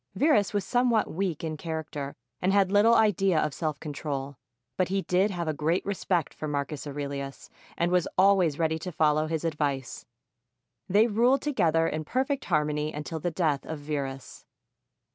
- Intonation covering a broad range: No, average, 4.6 semitones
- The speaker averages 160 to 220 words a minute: Yes, average, 165 wpm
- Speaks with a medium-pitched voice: Yes, medium, 160 Hz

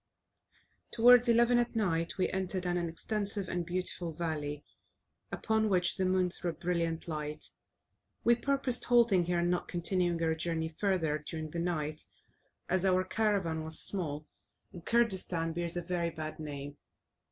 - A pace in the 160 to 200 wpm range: No, average, 150 wpm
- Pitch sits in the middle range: Yes, medium, 175 Hz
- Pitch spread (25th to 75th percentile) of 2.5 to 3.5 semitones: Yes, average, 3.1 semitones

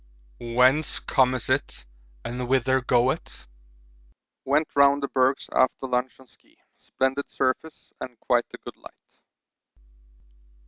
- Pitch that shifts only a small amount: Yes, narrow, 1.6 semitones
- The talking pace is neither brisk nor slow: No, slow, 120 wpm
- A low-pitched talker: Yes, low, 130 Hz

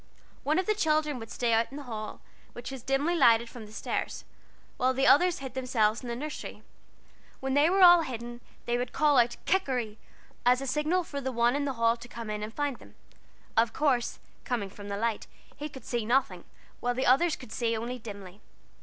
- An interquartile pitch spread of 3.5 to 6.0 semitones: Yes, average, 3.8 semitones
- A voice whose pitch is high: Yes, very high, 250 Hz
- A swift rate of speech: Yes, fast, 215 wpm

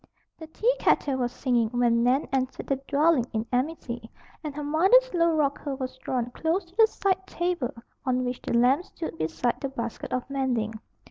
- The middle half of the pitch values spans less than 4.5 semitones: No, average, 4.9 semitones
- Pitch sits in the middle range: No, very high, 270 Hz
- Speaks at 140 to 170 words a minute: No, average, 180 wpm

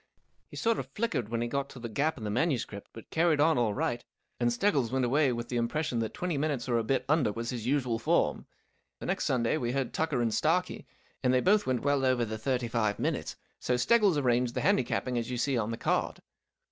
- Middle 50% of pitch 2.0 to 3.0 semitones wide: No, average, 3.7 semitones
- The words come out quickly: Yes, fast, 235 wpm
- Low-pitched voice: Yes, low, 125 Hz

